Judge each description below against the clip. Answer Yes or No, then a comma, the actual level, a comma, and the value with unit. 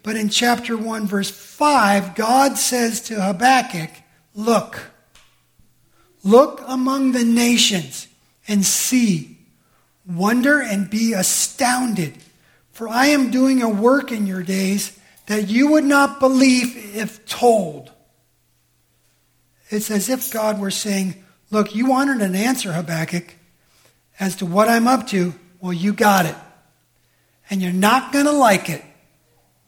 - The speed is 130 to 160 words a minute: Yes, slow, 135 wpm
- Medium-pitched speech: No, high, 210 Hz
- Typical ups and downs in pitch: Yes, average, 4.9 semitones